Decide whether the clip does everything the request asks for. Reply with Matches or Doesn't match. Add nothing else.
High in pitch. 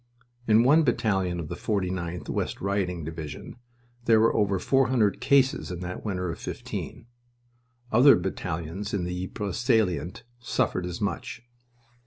Doesn't match